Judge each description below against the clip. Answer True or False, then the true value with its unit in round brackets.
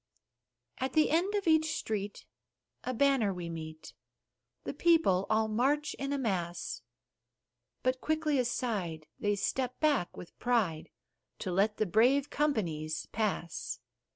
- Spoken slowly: True (130 wpm)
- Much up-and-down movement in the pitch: True (7.5 semitones)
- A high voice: True (225 Hz)